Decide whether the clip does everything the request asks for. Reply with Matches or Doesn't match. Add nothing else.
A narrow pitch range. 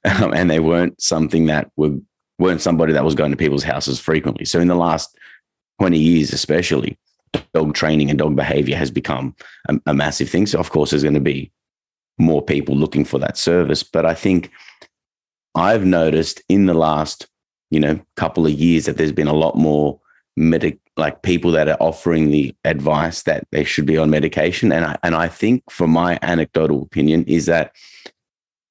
Matches